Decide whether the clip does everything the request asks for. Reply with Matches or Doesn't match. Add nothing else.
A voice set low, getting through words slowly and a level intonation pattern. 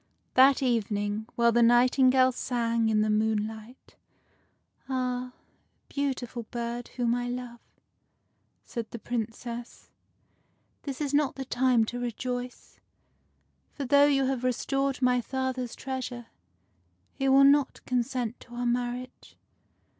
Doesn't match